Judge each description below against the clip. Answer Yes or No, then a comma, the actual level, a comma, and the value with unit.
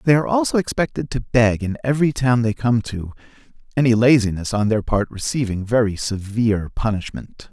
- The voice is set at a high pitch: No, low, 115 Hz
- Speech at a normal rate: Yes, average, 170 wpm